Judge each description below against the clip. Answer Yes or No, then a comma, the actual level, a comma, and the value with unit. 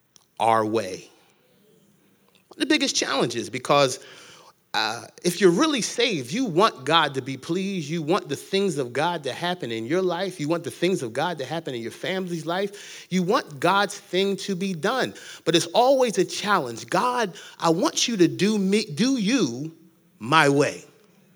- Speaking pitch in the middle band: Yes, medium, 180 Hz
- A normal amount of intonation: Yes, average, 3.5 semitones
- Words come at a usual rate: Yes, average, 185 wpm